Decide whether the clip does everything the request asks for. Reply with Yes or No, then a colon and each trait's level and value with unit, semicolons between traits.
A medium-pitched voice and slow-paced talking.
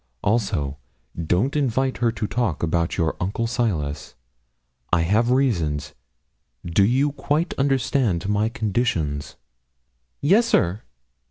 No: low, 110 Hz; slow, 110 wpm